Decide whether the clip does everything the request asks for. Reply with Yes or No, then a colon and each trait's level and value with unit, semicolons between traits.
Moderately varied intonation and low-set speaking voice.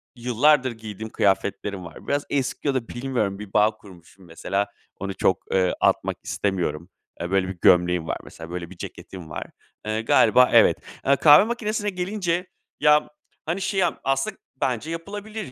No: wide, 7.9 semitones; low, 110 Hz